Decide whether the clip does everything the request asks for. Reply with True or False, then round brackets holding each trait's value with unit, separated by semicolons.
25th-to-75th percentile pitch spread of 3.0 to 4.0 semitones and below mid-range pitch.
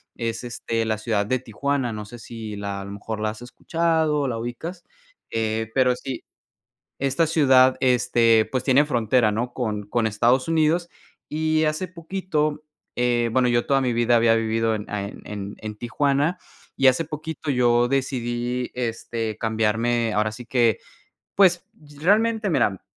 False (4.4 semitones; 120 Hz)